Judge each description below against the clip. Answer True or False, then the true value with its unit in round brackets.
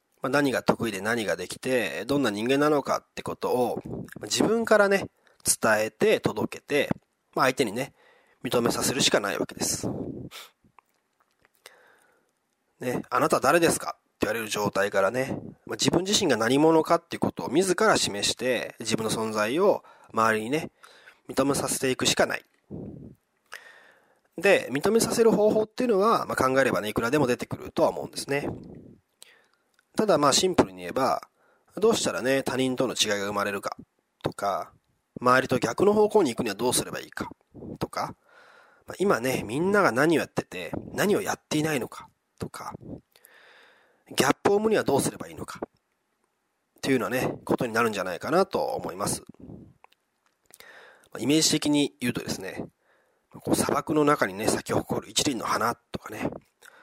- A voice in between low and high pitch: True (145 Hz)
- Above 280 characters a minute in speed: True (315 characters per minute)